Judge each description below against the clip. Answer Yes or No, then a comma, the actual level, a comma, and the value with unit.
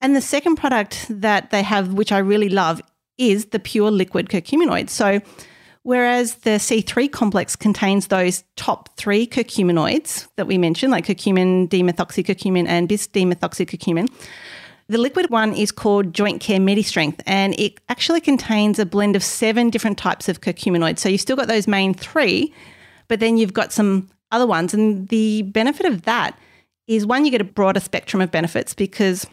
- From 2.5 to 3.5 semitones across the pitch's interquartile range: Yes, average, 3.1 semitones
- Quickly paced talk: No, average, 170 wpm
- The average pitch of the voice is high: Yes, high, 210 Hz